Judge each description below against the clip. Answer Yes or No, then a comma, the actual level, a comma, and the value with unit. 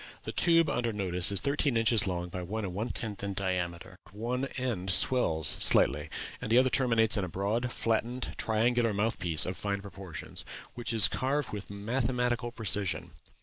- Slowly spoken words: No, average, 175 wpm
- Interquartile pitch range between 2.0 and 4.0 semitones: No, average, 4.4 semitones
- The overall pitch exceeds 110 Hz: No, low, 105 Hz